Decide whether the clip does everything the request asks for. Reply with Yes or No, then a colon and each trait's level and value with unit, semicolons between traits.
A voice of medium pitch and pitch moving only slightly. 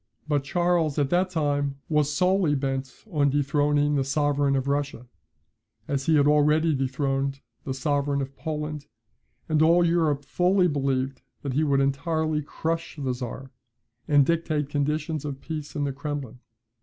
Yes: medium, 145 Hz; narrow, 2.2 semitones